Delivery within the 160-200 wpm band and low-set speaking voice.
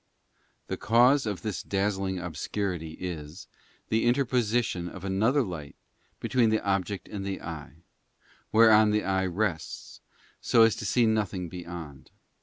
No: slow, 135 wpm; low, 100 Hz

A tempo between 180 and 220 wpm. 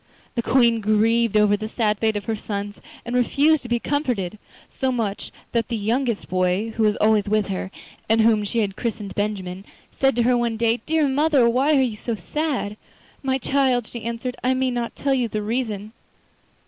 Yes: average, 200 wpm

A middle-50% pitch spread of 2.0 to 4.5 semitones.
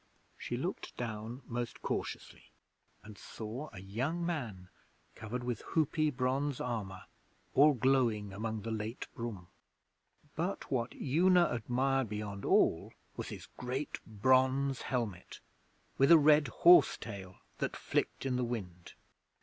Yes: average, 4.2 semitones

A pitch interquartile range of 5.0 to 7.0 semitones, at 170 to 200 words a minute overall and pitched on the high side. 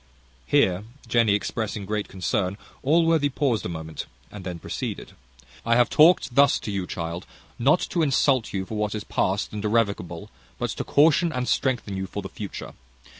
No: wide, 5.5 semitones; average, 175 wpm; low, 105 Hz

